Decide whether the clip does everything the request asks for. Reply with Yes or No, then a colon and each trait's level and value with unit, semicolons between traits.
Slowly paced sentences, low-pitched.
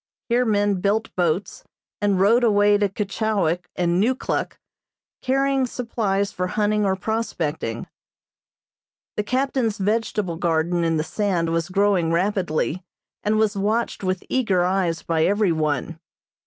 No: slow, 130 wpm; high, 200 Hz